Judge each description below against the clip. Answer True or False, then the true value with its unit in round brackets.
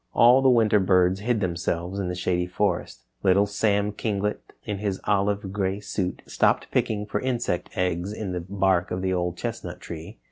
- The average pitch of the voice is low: True (95 Hz)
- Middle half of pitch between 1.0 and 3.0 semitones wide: True (2.5 semitones)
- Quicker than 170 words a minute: True (180 wpm)